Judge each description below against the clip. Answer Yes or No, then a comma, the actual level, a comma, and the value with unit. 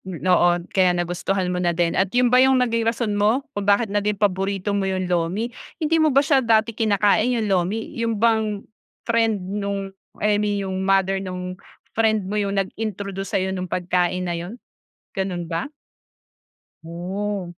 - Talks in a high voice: Yes, high, 200 Hz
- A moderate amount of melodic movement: Yes, average, 3.3 semitones